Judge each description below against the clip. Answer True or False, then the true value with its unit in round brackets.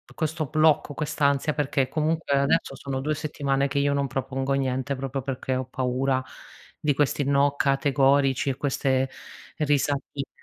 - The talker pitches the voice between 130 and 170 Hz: True (140 Hz)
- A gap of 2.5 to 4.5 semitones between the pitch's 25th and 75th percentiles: False (1.4 semitones)